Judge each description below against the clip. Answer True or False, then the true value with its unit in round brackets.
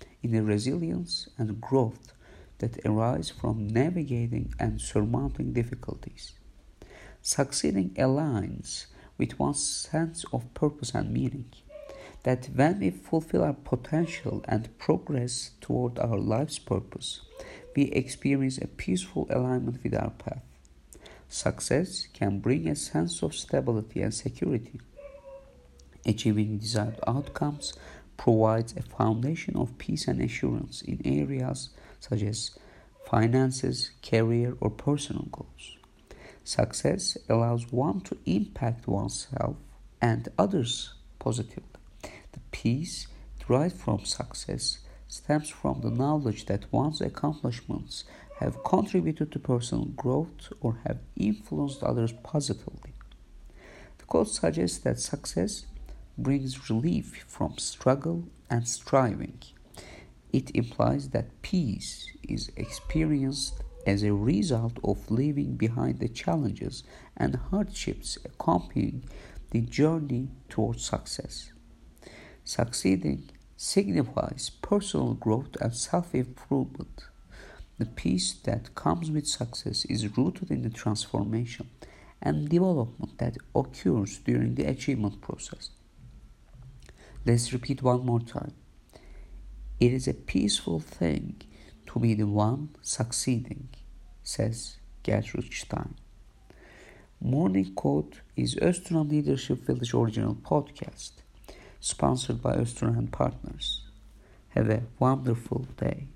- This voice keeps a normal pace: False (110 wpm)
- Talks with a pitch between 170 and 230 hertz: False (120 Hz)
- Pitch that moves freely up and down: False (4.7 semitones)